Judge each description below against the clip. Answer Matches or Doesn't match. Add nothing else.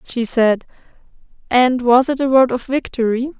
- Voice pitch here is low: Doesn't match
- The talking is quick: Doesn't match